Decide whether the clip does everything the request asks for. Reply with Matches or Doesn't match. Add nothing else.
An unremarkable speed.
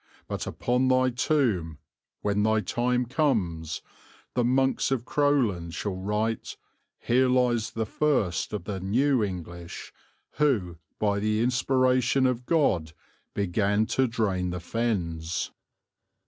Doesn't match